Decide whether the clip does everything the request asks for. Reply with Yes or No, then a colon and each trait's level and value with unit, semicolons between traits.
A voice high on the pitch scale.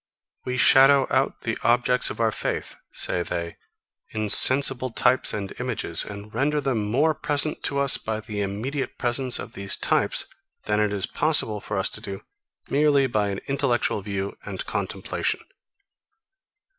No: low, 120 Hz